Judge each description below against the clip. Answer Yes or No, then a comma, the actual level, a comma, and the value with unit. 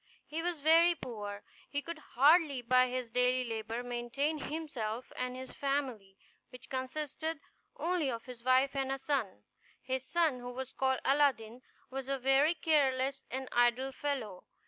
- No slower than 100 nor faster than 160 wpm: Yes, average, 155 wpm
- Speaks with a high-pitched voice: Yes, very high, 260 Hz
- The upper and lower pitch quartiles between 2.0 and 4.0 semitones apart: Yes, average, 2.8 semitones